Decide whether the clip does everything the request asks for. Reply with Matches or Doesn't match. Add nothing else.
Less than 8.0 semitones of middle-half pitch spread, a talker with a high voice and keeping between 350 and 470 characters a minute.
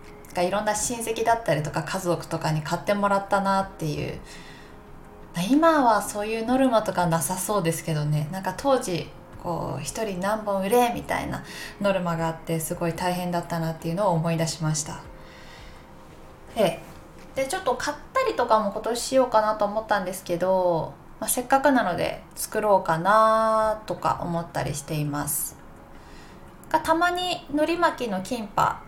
Doesn't match